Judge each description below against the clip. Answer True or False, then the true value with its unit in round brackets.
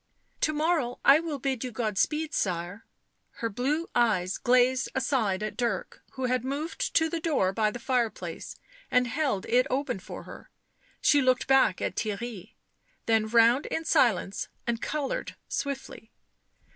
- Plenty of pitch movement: False (4.2 semitones)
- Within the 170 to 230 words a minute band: False (160 wpm)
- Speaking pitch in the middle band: False (250 Hz)